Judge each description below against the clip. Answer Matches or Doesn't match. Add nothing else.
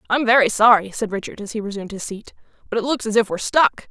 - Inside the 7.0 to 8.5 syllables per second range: Matches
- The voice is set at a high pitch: Matches